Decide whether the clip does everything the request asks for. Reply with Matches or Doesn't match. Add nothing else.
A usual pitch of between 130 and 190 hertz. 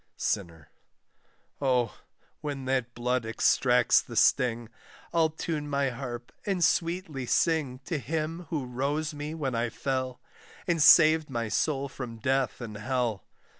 Matches